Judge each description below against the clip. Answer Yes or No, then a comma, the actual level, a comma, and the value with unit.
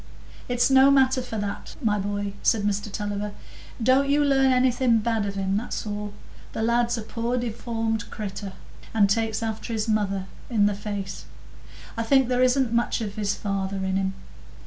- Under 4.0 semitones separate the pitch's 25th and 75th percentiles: Yes, average, 3.2 semitones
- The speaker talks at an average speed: Yes, average, 175 wpm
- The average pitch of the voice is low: No, high, 220 Hz